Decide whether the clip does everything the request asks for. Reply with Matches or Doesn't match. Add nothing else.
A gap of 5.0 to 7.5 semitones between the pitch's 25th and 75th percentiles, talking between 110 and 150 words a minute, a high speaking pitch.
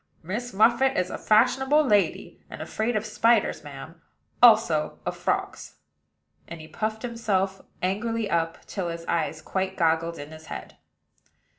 Matches